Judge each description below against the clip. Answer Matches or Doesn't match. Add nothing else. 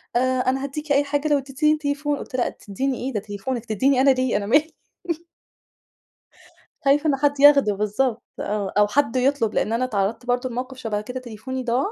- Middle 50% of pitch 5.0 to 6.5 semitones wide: Doesn't match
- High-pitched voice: Matches